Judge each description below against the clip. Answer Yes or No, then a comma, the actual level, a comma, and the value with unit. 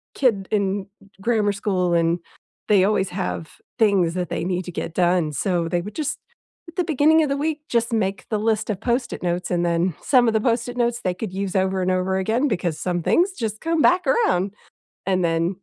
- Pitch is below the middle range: No, high, 195 Hz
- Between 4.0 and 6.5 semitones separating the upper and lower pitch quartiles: Yes, average, 4.7 semitones